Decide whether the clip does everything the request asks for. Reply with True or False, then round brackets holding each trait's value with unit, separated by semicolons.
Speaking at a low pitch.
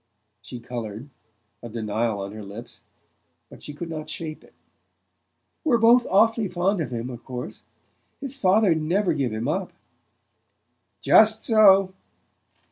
False (155 Hz)